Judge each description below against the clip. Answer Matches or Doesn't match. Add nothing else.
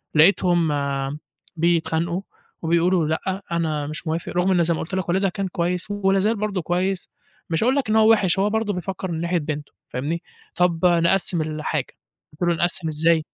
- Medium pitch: Matches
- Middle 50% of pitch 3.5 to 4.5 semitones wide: Doesn't match